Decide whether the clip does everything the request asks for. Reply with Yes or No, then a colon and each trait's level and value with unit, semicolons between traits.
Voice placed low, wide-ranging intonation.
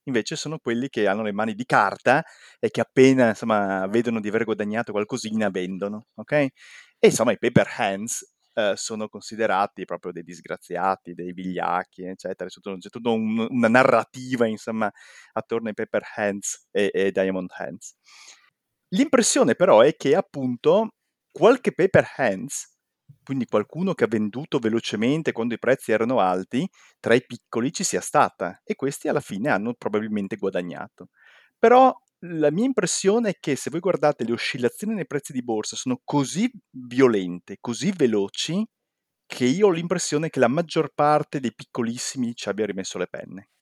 Yes: low, 120 Hz; wide, 6.5 semitones